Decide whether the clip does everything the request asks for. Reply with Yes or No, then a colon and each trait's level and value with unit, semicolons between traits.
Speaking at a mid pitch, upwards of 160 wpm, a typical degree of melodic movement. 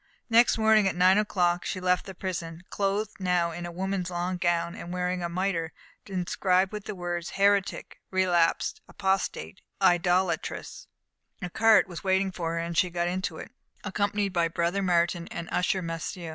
No: medium, 180 Hz; average, 175 wpm; narrow, 2.0 semitones